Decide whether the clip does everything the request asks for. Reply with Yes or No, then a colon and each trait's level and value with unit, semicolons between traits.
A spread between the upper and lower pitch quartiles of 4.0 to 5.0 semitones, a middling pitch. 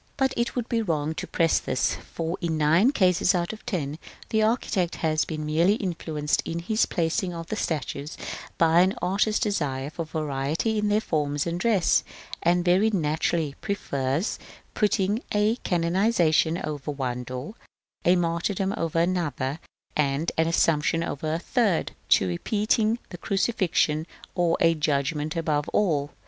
Yes: average, 4.6 semitones; medium, 165 Hz